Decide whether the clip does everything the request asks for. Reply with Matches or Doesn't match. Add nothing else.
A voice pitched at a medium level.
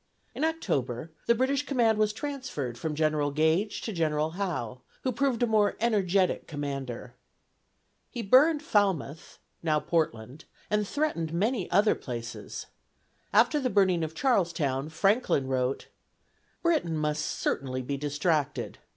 Matches